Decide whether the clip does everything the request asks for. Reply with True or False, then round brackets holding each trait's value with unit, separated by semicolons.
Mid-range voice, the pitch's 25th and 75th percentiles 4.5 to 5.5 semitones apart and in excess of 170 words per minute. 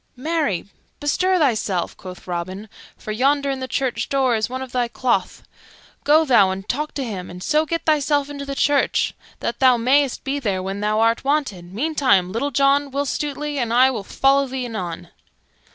False (260 Hz; 5.1 semitones; 185 wpm)